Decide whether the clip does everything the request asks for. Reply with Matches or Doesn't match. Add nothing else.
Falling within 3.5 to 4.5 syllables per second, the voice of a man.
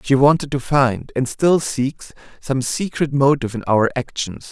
Matches